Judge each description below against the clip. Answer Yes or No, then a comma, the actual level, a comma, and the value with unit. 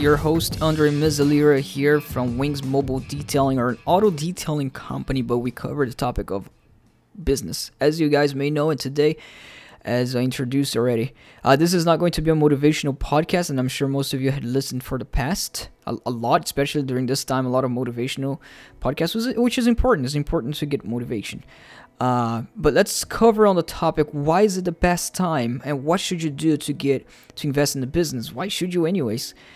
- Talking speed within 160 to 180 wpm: No, fast, 205 wpm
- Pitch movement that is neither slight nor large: Yes, average, 3.8 semitones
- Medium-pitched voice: Yes, medium, 145 Hz